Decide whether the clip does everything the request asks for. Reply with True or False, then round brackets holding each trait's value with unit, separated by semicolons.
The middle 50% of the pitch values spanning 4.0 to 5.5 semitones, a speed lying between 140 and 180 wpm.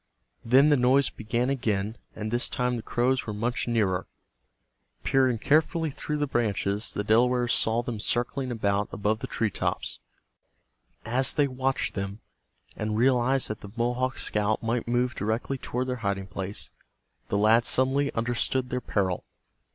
False (3.3 semitones; 155 wpm)